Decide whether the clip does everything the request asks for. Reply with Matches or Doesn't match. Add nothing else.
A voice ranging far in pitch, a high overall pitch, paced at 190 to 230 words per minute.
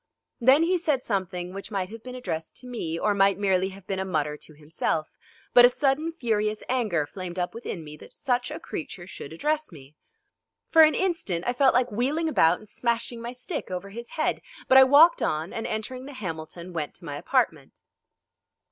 Matches